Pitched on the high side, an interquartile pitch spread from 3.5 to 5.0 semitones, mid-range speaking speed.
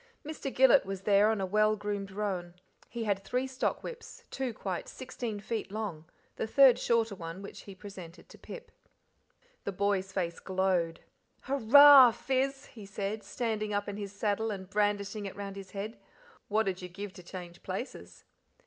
No: high, 205 Hz; average, 2.8 semitones; average, 175 wpm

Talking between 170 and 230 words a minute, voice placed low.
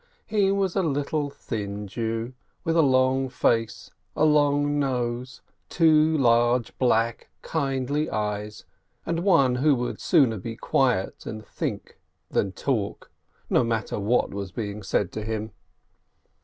No: average, 140 wpm; low, 125 Hz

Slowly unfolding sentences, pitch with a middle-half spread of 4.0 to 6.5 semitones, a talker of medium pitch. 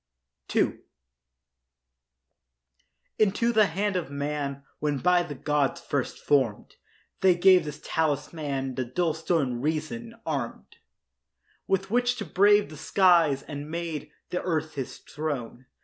Yes: slow, 125 wpm; average, 4.3 semitones; medium, 155 Hz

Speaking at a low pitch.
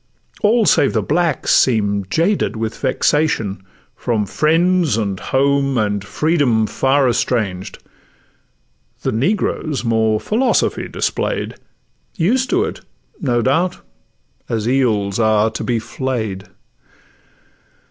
Yes: low, 125 Hz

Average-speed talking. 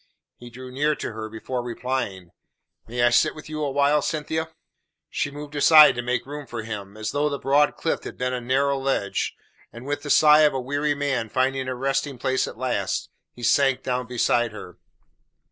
Yes: average, 195 wpm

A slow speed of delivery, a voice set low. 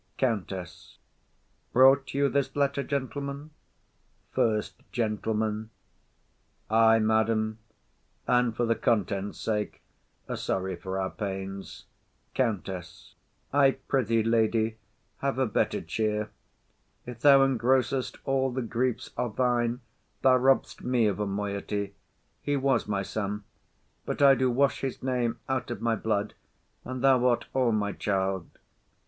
Yes: slow, 130 wpm; low, 115 Hz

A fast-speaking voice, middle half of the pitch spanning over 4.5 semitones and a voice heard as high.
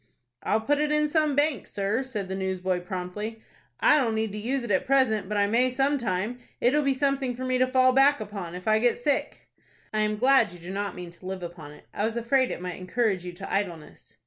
Yes: fast, 240 wpm; wide, 5.5 semitones; high, 220 Hz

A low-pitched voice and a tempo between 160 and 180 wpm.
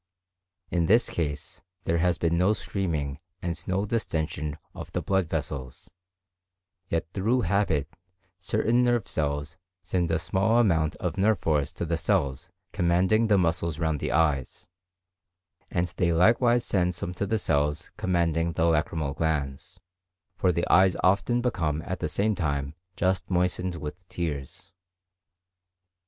No: very low, 85 Hz; average, 145 wpm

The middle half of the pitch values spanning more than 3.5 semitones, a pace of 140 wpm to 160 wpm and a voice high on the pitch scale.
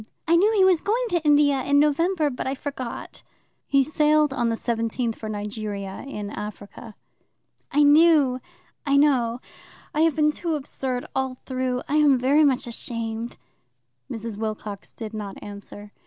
Yes: average, 4.9 semitones; average, 155 wpm; very high, 260 Hz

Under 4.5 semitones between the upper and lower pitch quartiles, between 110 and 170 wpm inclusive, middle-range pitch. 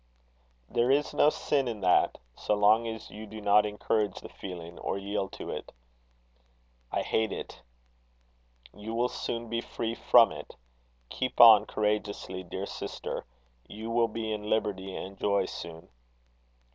No: narrow, 2.6 semitones; average, 150 wpm; low, 105 Hz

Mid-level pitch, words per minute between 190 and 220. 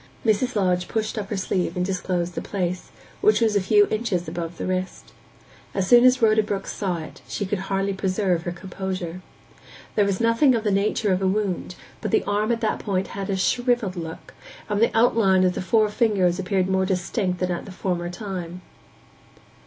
No: high, 195 Hz; average, 200 wpm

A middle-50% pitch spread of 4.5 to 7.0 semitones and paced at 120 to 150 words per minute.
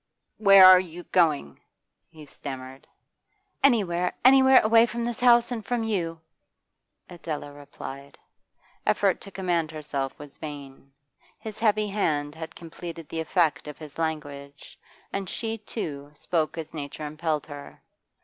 Yes: wide, 5.5 semitones; slow, 135 wpm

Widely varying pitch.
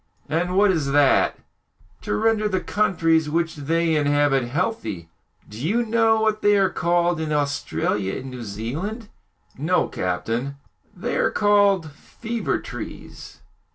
Yes: wide, 6.8 semitones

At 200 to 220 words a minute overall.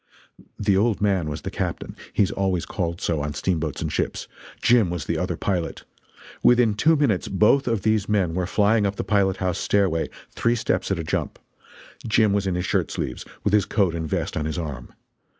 Yes: fast, 205 wpm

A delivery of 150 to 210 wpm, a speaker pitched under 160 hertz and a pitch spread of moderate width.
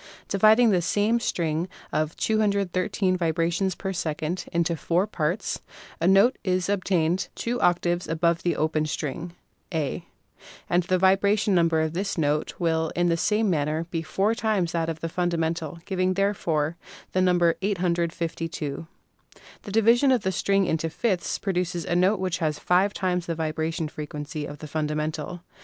No: average, 160 wpm; medium, 175 Hz; average, 3.0 semitones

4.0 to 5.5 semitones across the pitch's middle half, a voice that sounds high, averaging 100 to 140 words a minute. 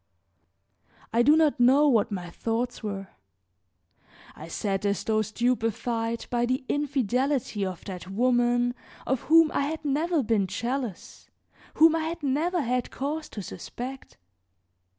Yes: average, 4.9 semitones; high, 245 Hz; slow, 135 wpm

